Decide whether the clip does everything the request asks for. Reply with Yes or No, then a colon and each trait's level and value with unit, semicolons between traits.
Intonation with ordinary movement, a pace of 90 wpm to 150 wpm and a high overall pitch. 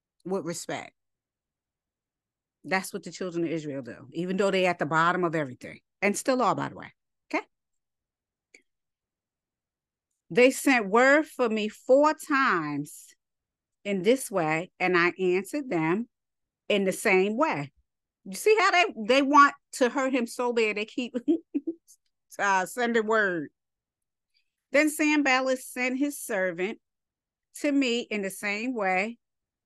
No: wide, 6.9 semitones; average, 145 wpm; high, 205 Hz